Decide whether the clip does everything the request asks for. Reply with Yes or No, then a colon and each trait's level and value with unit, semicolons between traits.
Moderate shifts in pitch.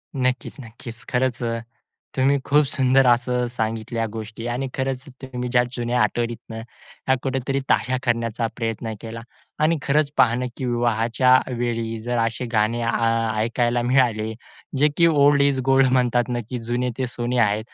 No: narrow, 2.2 semitones